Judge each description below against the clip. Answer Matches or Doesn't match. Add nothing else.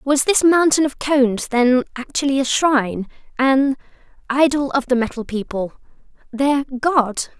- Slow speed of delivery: Matches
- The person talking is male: Doesn't match